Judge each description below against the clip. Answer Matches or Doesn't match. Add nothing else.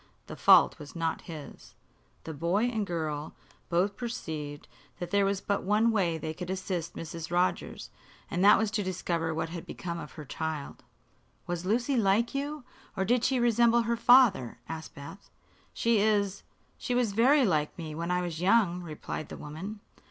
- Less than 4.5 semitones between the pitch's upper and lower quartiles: Doesn't match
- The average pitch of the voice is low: Doesn't match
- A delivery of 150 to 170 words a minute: Doesn't match